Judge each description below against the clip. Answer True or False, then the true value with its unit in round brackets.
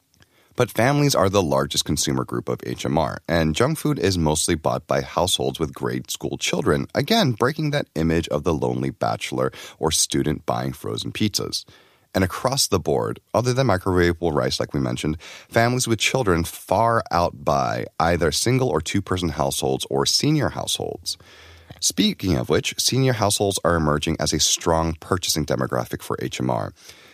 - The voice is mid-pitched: False (85 Hz)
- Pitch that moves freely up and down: True (7.6 semitones)